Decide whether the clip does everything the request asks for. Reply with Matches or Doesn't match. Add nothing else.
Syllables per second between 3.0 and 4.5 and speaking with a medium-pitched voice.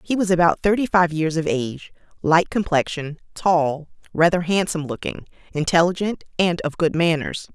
Doesn't match